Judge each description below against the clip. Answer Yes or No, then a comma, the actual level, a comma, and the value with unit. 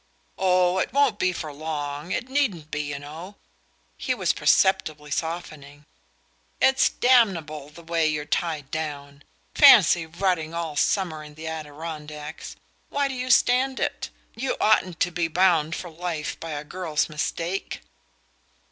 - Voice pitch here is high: No, medium, 165 Hz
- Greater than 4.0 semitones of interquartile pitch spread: No, average, 3.7 semitones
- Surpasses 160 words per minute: No, average, 145 wpm